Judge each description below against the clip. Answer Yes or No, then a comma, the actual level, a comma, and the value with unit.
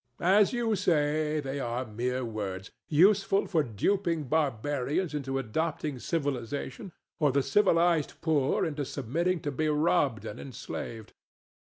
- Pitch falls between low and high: Yes, medium, 145 Hz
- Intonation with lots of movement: No, average, 4.7 semitones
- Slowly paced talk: Yes, slow, 130 wpm